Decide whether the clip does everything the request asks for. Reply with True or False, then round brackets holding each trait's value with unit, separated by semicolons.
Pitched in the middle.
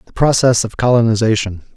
False (115 Hz)